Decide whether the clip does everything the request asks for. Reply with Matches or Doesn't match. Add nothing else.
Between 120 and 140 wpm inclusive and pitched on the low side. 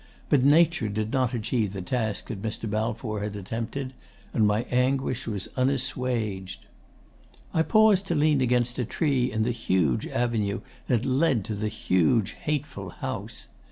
Doesn't match